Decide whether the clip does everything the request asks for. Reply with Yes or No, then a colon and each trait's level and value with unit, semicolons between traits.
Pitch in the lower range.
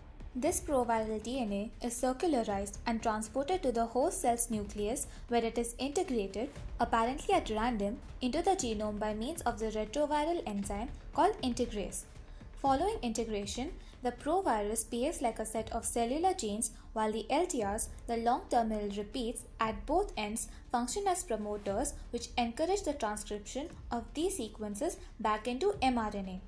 No: high, 235 Hz